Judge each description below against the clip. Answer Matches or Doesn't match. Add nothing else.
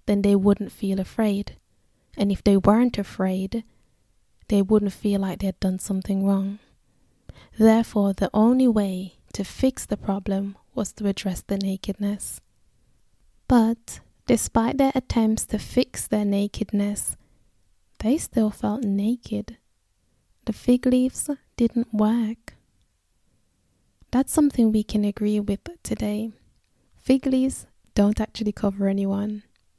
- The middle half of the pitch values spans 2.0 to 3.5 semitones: Matches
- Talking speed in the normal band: Doesn't match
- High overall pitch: Matches